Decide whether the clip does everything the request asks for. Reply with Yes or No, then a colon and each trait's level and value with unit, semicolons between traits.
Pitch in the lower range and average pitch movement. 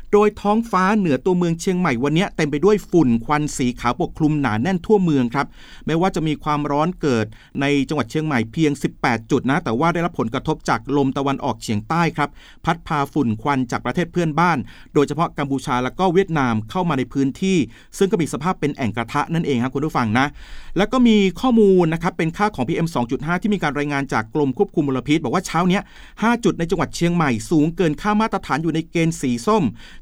No: medium, 155 Hz; average, 4.7 semitones